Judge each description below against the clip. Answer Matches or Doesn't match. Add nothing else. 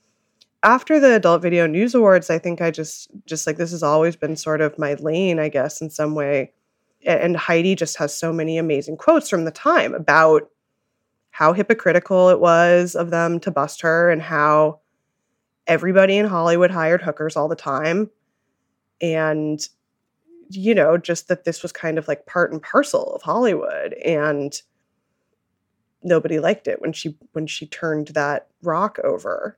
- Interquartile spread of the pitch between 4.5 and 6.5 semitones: Doesn't match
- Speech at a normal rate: Matches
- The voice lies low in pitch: Doesn't match